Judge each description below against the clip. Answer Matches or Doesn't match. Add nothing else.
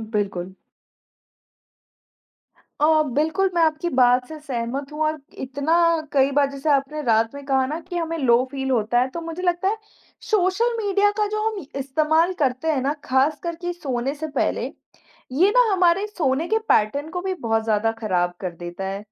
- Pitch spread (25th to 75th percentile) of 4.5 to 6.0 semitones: Matches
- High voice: Matches